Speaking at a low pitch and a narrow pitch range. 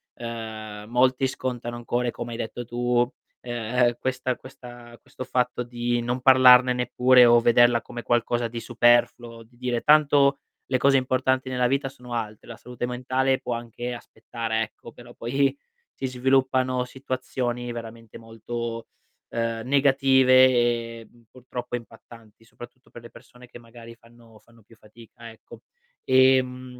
Yes: low, 120 Hz; narrow, 1.6 semitones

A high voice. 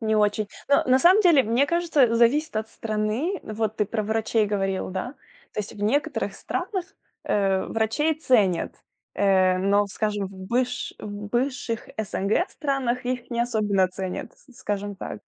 Yes: high, 220 Hz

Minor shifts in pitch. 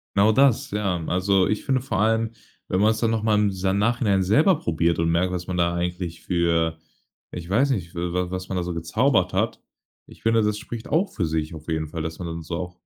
No: average, 4.3 semitones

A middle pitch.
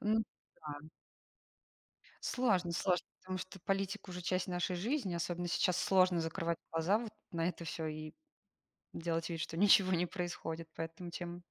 Yes: medium, 175 Hz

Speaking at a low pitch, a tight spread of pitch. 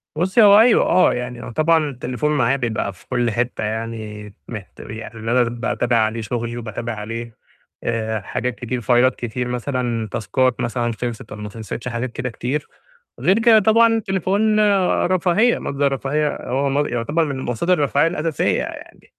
No: low, 125 Hz; average, 4.7 semitones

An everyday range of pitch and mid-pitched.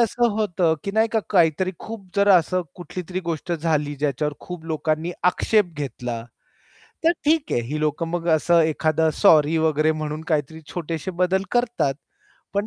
Yes: average, 3.8 semitones; medium, 165 Hz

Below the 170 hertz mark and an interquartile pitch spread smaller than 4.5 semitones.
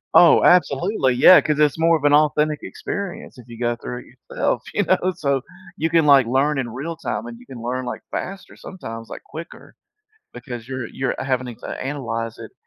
No: medium, 140 Hz; average, 4.9 semitones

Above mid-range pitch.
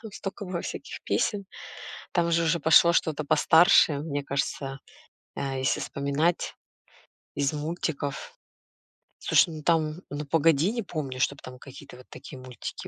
No: medium, 155 Hz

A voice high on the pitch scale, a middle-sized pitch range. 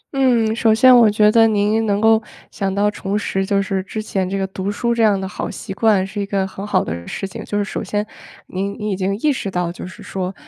No: high, 205 Hz; narrow, 2.3 semitones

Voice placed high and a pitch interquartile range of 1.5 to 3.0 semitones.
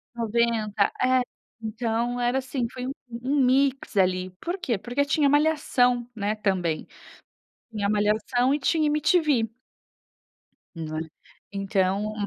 No: high, 240 Hz; average, 4.4 semitones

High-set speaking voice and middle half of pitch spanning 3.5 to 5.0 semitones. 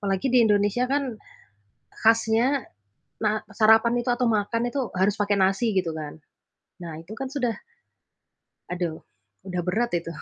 Yes: high, 215 Hz; average, 4.2 semitones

